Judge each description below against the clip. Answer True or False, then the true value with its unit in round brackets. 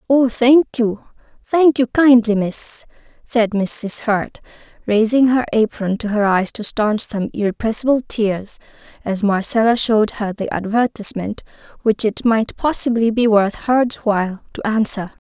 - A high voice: True (225 Hz)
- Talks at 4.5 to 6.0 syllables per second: False (4.3 syllables/s)